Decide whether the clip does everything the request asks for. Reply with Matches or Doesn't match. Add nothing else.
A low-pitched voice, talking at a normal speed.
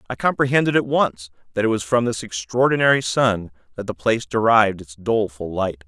Matches